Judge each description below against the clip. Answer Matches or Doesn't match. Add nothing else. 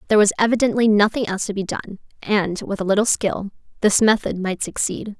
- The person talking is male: Doesn't match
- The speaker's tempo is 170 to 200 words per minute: Matches